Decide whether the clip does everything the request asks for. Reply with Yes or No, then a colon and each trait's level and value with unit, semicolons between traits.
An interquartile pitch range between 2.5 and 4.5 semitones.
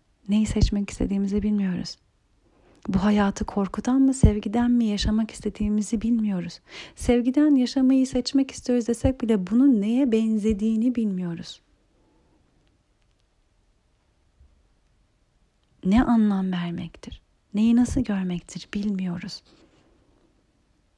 Yes: average, 3.9 semitones